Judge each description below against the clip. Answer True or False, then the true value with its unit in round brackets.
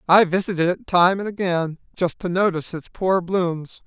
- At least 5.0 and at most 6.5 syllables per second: True (5.2 syllables/s)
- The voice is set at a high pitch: False (180 Hz)